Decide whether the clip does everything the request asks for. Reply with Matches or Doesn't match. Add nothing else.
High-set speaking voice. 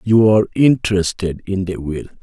Doesn't match